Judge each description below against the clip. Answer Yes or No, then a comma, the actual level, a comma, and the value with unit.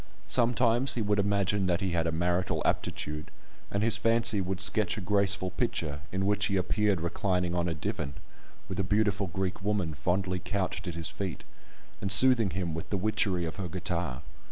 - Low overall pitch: Yes, very low, 95 Hz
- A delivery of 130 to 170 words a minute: No, average, 185 wpm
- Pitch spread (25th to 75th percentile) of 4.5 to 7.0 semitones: No, average, 2.8 semitones